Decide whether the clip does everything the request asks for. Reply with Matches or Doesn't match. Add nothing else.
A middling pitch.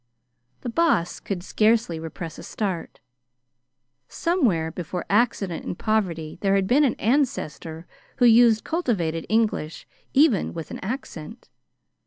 Doesn't match